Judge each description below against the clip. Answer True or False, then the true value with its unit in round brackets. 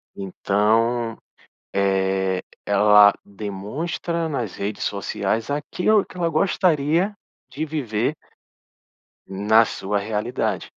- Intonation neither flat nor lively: False (6.8 semitones)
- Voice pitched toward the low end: True (110 Hz)